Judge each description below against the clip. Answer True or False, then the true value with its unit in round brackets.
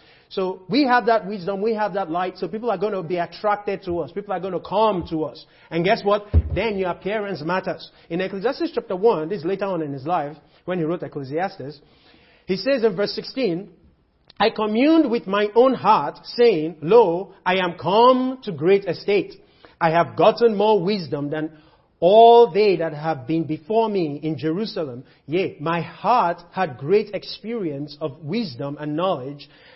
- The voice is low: False (185 Hz)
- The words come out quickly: False (185 wpm)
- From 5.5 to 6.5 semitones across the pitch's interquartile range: False (5.1 semitones)